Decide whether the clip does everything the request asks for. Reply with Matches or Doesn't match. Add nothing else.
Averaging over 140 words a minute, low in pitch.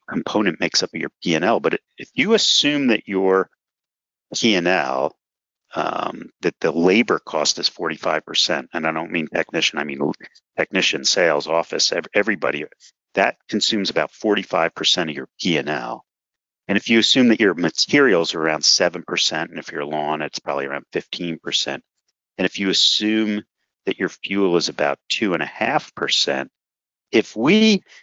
Matches